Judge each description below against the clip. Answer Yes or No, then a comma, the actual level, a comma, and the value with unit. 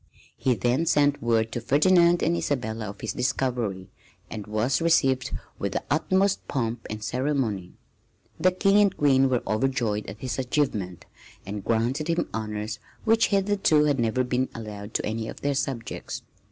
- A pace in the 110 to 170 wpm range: Yes, average, 160 wpm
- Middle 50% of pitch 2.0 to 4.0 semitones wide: No, average, 5.2 semitones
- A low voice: Yes, low, 125 Hz